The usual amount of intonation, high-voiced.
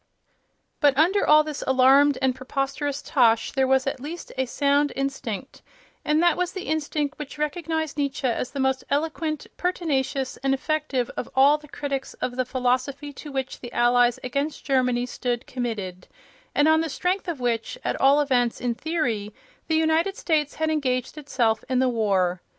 Yes: average, 3.3 semitones; very high, 275 Hz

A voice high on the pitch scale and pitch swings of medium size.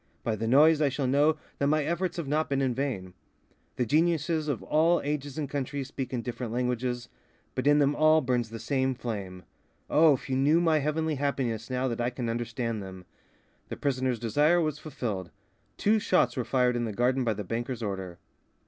No: low, 130 Hz; average, 4.1 semitones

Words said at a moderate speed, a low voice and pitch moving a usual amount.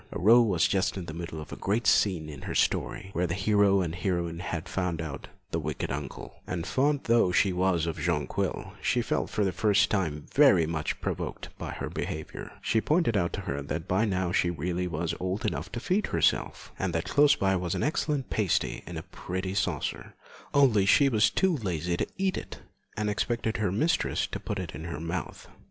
No: fast, 210 wpm; very low, 95 Hz; average, 4.3 semitones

